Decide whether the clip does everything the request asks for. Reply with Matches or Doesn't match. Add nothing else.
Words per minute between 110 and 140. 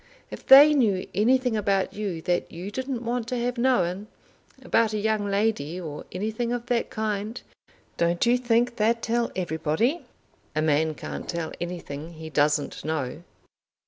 Doesn't match